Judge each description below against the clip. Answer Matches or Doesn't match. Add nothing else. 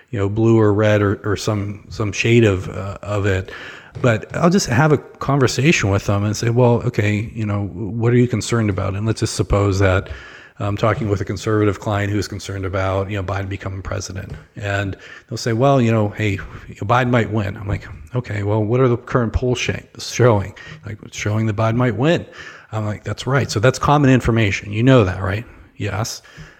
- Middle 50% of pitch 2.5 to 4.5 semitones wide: Matches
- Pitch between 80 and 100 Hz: Doesn't match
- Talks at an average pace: Doesn't match